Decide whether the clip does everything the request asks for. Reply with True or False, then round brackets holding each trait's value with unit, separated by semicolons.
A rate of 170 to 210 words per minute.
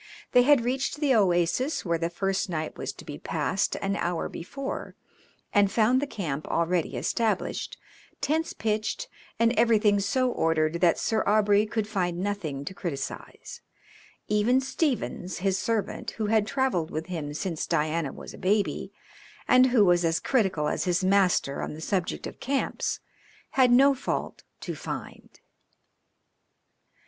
False (150 wpm)